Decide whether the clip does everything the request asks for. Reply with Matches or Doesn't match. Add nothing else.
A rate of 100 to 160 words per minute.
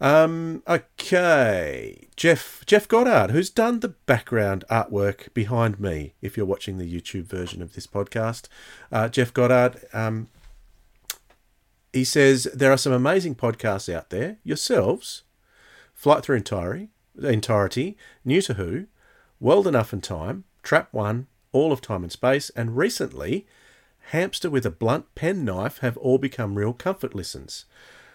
Matches